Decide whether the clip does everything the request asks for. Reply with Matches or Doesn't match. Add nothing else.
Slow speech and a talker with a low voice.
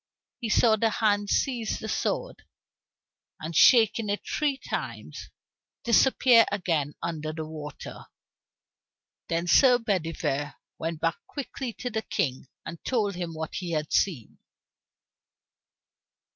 Doesn't match